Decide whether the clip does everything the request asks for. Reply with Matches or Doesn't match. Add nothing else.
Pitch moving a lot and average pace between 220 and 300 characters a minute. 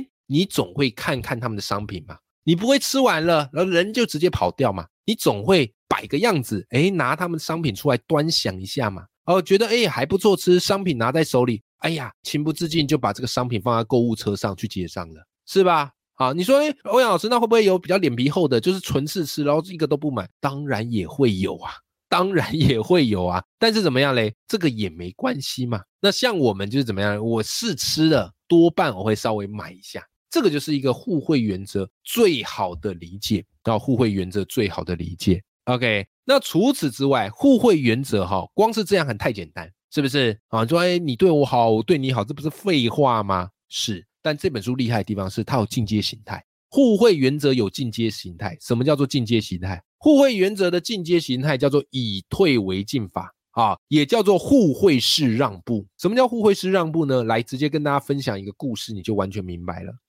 Doesn't match